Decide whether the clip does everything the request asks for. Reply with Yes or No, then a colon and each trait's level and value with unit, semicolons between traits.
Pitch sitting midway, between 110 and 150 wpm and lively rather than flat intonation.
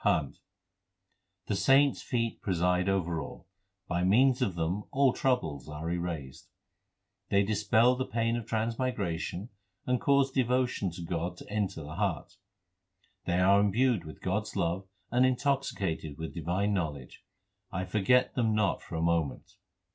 No: low, 100 Hz; average, 145 wpm; wide, 6.0 semitones